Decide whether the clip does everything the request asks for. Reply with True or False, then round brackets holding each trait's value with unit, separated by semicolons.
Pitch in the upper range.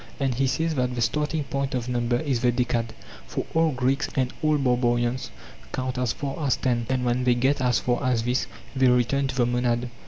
False (125 Hz)